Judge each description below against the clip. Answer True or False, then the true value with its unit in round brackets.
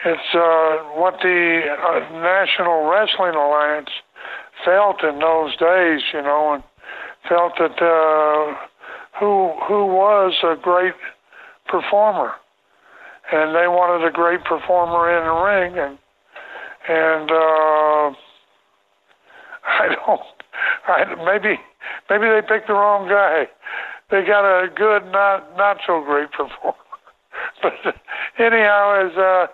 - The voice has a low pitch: False (170 Hz)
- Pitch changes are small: False (4.0 semitones)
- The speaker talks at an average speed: False (120 wpm)